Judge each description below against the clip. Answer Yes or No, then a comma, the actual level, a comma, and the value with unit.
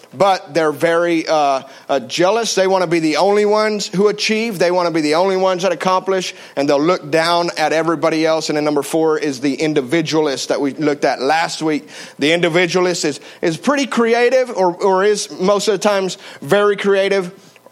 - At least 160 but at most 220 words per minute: Yes, average, 200 wpm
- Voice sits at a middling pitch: Yes, medium, 180 Hz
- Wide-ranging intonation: No, average, 4.0 semitones